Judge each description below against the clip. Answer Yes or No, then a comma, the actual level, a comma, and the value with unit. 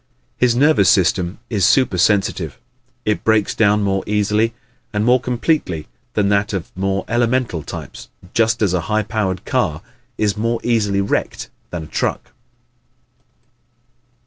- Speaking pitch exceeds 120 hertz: No, low, 105 Hz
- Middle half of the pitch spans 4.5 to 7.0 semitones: No, average, 3.0 semitones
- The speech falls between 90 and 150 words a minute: Yes, average, 140 wpm